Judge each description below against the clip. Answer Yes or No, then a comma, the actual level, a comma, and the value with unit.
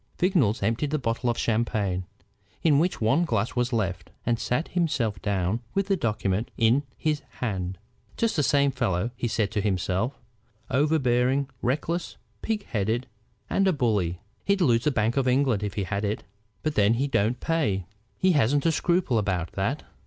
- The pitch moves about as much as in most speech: No, wide, 6.0 semitones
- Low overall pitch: Yes, low, 120 Hz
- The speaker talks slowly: No, average, 175 wpm